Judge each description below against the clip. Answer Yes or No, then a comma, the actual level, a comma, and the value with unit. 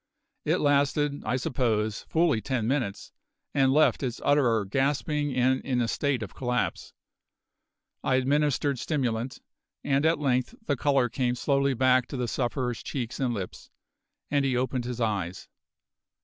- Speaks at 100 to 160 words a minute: Yes, average, 150 wpm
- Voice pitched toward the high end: No, low, 130 Hz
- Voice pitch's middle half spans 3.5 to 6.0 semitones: No, average, 2.7 semitones